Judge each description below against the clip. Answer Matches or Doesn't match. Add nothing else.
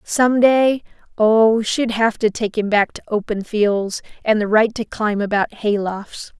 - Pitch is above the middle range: Matches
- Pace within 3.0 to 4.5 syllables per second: Matches